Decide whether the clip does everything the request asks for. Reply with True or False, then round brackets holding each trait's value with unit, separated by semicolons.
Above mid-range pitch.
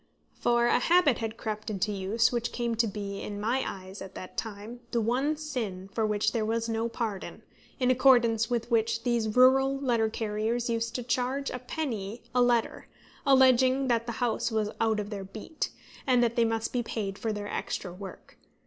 True (230 Hz)